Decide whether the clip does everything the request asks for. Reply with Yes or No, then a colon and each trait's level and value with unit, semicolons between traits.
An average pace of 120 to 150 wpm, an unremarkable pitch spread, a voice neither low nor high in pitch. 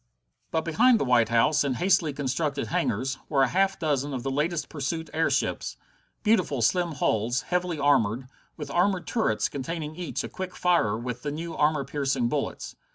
No: average, 170 wpm; average, 4.5 semitones; medium, 150 Hz